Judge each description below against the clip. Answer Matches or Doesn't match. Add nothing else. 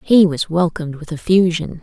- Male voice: Doesn't match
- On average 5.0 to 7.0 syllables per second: Matches